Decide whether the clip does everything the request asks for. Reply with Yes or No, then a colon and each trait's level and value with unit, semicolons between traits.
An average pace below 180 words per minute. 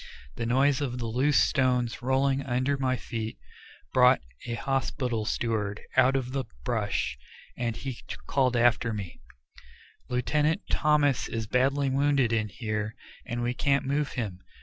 Yes: average, 145 wpm